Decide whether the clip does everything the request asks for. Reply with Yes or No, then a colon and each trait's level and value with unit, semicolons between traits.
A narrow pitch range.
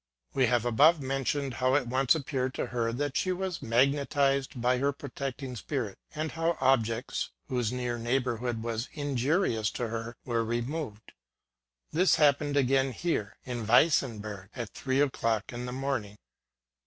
No: average, 3.2 semitones